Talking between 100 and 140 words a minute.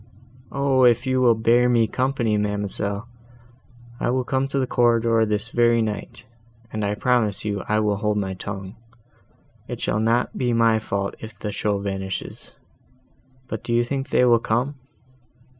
No: average, 160 wpm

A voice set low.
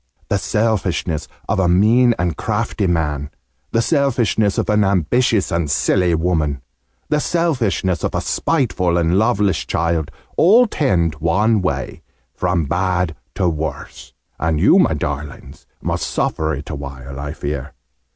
Yes: very low, 90 Hz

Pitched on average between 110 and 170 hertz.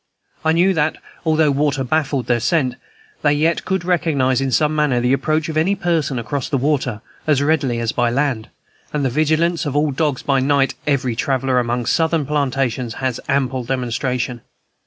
Yes: medium, 140 Hz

